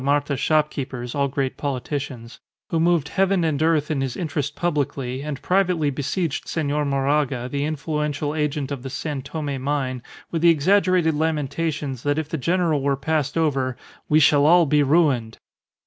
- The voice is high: No, medium, 145 Hz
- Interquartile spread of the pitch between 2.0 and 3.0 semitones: Yes, narrow, 2.6 semitones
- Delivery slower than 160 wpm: No, average, 165 wpm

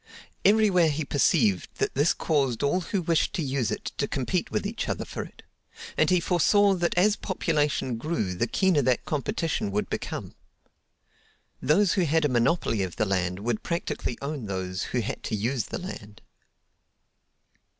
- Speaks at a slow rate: No, average, 170 wpm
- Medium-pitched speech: Yes, medium, 145 Hz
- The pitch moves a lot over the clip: Yes, wide, 7.3 semitones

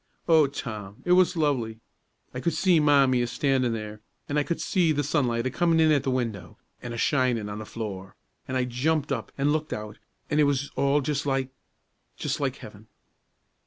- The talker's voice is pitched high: No, low, 135 Hz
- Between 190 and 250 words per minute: Yes, average, 200 wpm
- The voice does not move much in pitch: No, average, 4.2 semitones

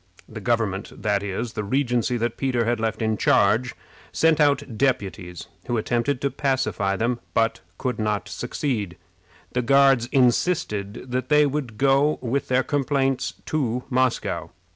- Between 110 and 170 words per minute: Yes, average, 145 wpm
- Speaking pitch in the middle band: No, low, 120 Hz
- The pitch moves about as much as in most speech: Yes, average, 3.9 semitones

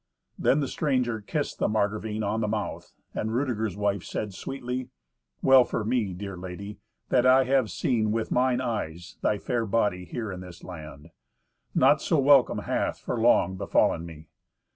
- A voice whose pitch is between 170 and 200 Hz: No, low, 110 Hz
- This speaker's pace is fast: No, average, 165 wpm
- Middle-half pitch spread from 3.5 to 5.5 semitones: Yes, average, 4.4 semitones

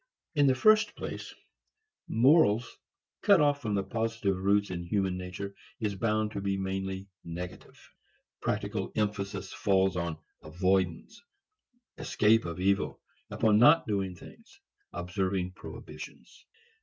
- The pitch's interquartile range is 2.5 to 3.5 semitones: Yes, average, 3.2 semitones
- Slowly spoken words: Yes, slow, 120 wpm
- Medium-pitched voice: No, low, 100 Hz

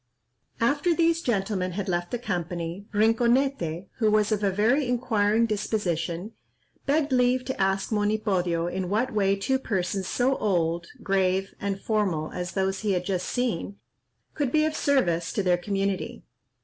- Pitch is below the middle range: No, high, 205 Hz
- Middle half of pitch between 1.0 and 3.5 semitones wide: No, average, 4.8 semitones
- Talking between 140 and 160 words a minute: Yes, average, 155 wpm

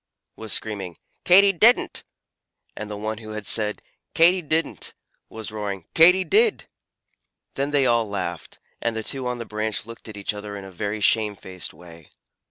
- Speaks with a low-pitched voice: Yes, low, 110 Hz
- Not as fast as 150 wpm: No, average, 170 wpm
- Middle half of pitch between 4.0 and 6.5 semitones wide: Yes, average, 5.0 semitones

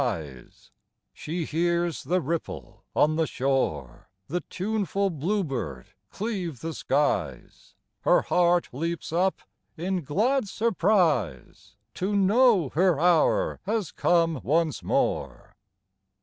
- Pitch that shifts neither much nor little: Yes, average, 5.0 semitones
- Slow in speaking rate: Yes, slow, 115 wpm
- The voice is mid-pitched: Yes, medium, 170 Hz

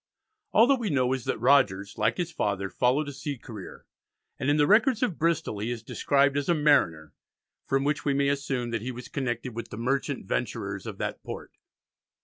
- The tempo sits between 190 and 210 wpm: Yes, fast, 205 wpm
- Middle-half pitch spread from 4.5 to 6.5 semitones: No, average, 3.9 semitones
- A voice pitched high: No, low, 135 Hz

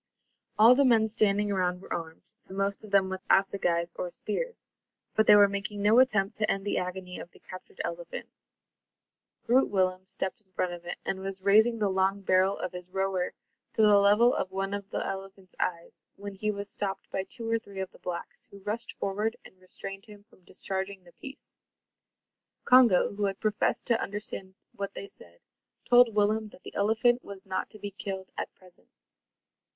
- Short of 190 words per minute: No, average, 195 wpm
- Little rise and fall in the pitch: Yes, narrow, 2.1 semitones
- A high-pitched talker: Yes, high, 200 Hz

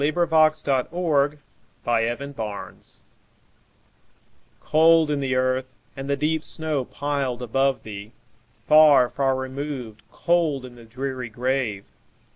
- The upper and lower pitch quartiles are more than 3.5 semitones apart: No, average, 3.2 semitones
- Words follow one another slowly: Yes, slow, 105 wpm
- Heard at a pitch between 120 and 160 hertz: Yes, low, 135 Hz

